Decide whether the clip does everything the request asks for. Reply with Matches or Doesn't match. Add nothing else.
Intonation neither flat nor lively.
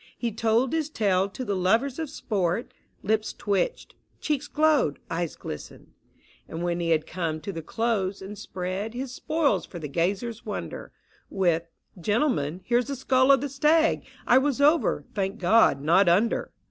Doesn't match